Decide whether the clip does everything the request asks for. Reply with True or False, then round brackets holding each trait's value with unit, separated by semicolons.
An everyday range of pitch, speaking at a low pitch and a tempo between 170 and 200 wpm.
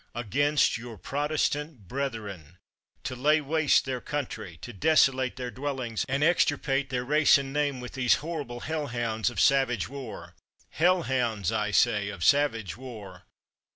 False (4.2 semitones; 130 Hz; 155 wpm)